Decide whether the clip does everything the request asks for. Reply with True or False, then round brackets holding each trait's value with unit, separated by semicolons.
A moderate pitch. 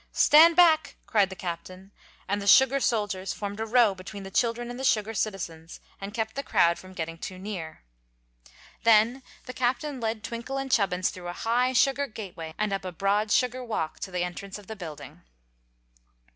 False (210 Hz)